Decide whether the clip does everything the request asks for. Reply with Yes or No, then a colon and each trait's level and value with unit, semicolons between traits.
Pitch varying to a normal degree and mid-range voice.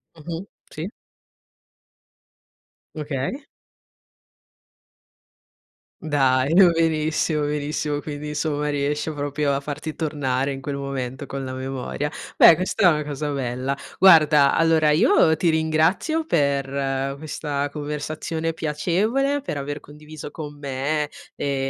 No: narrow, 2.3 semitones; medium, 150 Hz